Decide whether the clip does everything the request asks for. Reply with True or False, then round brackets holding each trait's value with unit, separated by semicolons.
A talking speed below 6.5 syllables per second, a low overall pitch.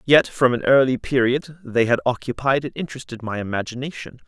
True (5.8 syllables/s; 130 Hz)